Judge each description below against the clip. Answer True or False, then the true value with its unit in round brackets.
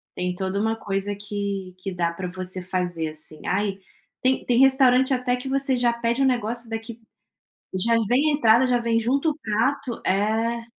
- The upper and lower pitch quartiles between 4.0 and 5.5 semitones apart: True (4.5 semitones)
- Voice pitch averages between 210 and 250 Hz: True (225 Hz)